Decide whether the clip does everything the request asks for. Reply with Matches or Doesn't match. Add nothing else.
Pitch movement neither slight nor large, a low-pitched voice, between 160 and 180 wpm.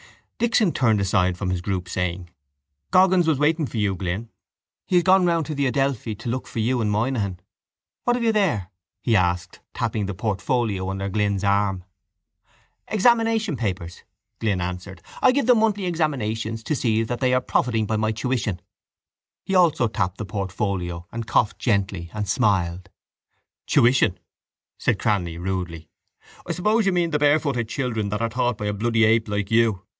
Doesn't match